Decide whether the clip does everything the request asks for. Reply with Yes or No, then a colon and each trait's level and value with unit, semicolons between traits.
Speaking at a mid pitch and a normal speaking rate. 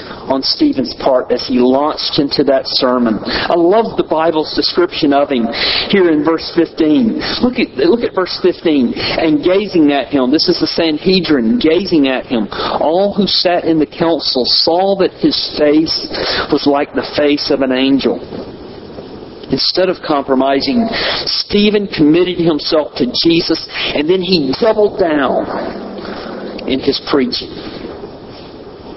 Yes: medium, 165 Hz; average, 145 wpm